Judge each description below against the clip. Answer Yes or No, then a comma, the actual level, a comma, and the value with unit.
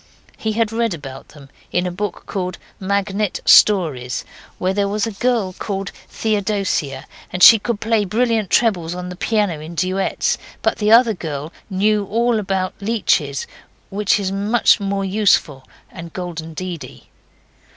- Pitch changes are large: No, average, 3.2 semitones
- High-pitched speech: Yes, high, 195 Hz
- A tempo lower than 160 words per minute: Yes, average, 150 wpm